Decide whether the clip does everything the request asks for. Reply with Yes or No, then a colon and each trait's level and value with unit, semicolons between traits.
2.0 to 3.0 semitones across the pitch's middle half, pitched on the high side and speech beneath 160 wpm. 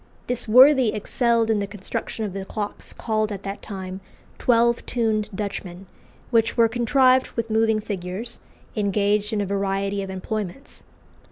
Yes: narrow, 2.6 semitones; high, 215 Hz; average, 150 wpm